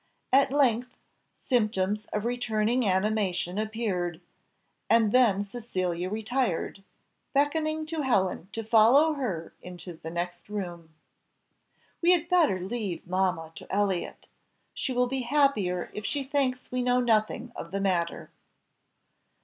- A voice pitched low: No, high, 215 Hz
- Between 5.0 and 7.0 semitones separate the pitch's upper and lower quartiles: Yes, wide, 5.4 semitones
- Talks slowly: Yes, slow, 125 wpm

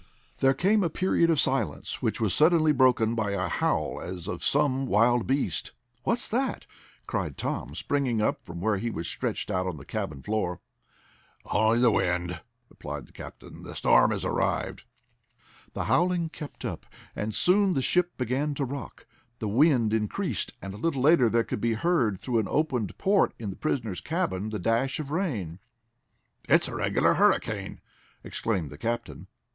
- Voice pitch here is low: Yes, low, 120 Hz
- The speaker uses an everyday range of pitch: No, wide, 6.7 semitones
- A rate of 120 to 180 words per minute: Yes, average, 175 wpm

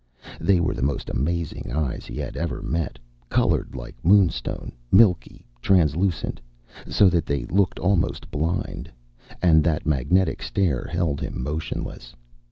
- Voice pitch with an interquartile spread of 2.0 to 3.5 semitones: No, average, 4.0 semitones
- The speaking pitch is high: No, very low, 85 Hz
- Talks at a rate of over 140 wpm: No, slow, 135 wpm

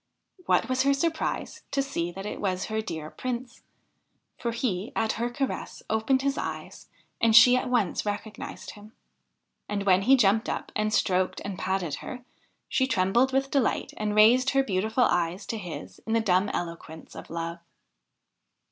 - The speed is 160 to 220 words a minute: Yes, average, 170 wpm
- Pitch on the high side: Yes, high, 220 Hz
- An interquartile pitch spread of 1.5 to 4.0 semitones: No, average, 5.1 semitones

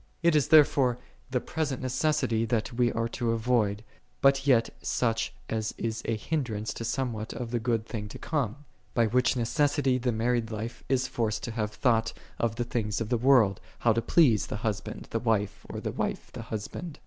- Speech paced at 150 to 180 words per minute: No, average, 195 wpm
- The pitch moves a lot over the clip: No, narrow, 2.6 semitones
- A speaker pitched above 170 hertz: No, low, 115 Hz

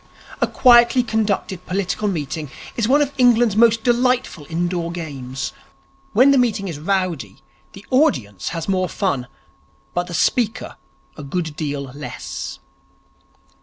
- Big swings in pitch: Yes, wide, 7.3 semitones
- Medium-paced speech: No, slow, 130 wpm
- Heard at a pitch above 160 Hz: Yes, medium, 185 Hz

